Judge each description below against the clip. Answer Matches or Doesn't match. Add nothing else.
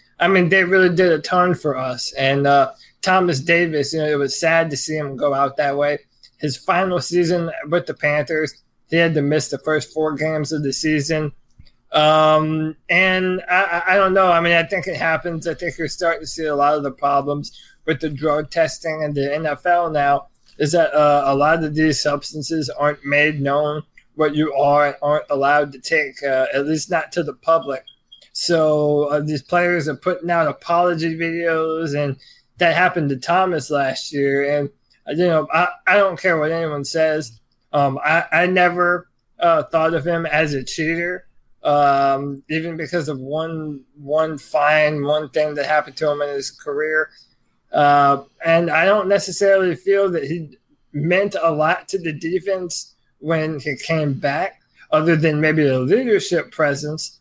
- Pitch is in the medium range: Matches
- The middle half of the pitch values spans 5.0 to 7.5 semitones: Doesn't match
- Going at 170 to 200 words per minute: Matches